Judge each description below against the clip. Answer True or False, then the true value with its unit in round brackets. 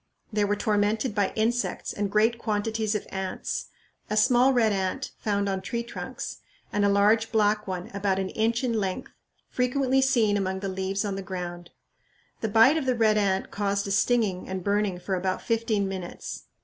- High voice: True (205 Hz)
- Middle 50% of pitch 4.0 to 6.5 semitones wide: False (2.7 semitones)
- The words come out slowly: False (185 wpm)